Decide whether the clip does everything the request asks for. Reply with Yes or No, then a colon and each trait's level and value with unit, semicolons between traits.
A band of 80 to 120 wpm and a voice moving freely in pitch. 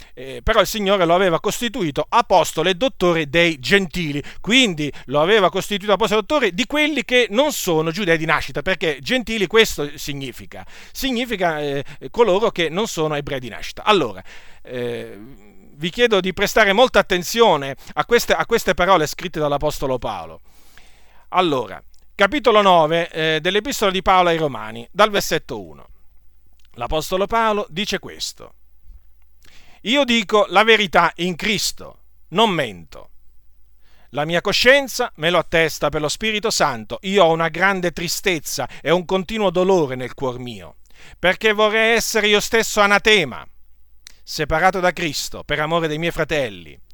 No: average, 145 wpm; wide, 6.1 semitones